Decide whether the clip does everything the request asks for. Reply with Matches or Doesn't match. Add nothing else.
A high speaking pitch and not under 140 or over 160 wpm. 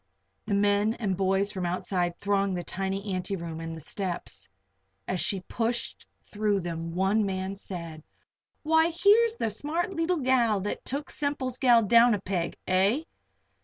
Matches